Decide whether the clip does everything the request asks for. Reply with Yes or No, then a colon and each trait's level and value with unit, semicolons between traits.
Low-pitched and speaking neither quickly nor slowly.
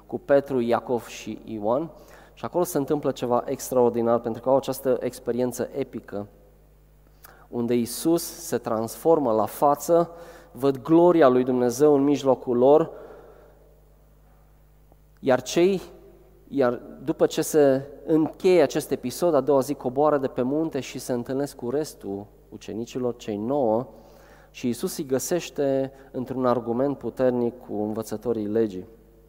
Yes: low, 130 Hz; average, 130 wpm